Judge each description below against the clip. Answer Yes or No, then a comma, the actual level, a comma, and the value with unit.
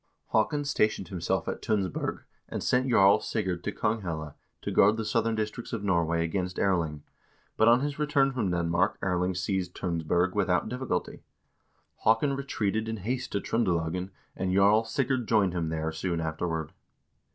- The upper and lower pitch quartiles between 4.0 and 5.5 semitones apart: Yes, average, 4.4 semitones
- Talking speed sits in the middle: Yes, average, 160 wpm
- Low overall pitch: Yes, very low, 95 Hz